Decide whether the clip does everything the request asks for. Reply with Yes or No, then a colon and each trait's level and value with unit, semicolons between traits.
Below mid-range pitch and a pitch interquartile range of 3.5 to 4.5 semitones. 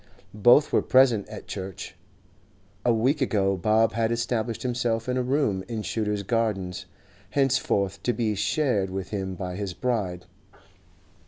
Yes: low, 110 Hz; average, 4.0 semitones